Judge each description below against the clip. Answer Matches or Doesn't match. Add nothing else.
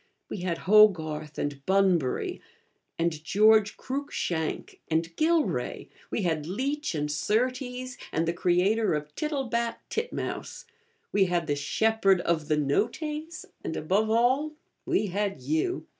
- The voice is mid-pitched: Doesn't match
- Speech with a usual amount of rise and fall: Doesn't match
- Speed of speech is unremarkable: Doesn't match